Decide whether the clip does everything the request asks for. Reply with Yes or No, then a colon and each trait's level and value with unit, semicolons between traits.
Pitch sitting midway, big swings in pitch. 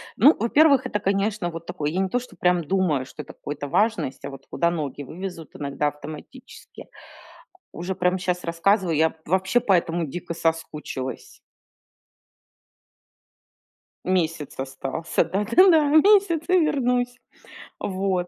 Yes: medium, 180 Hz; wide, 5.7 semitones